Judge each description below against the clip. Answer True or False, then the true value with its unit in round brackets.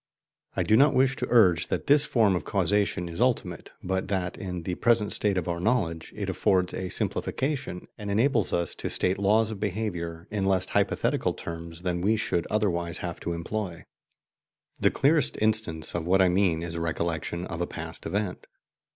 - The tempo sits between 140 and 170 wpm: False (185 wpm)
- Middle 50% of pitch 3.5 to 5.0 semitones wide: True (4.0 semitones)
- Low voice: True (95 Hz)